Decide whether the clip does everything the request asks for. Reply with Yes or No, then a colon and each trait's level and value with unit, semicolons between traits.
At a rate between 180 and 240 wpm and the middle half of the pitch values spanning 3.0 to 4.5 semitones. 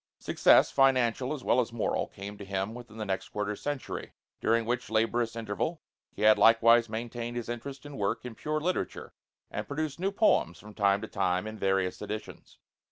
Yes: average, 185 wpm; average, 3.4 semitones